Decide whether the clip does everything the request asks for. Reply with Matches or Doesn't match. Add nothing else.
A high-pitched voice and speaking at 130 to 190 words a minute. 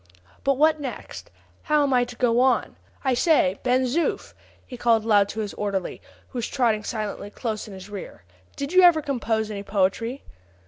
Matches